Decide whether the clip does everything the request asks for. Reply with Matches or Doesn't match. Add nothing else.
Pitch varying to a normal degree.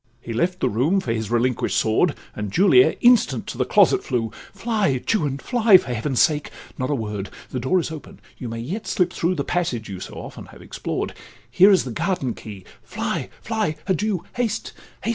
Doesn't match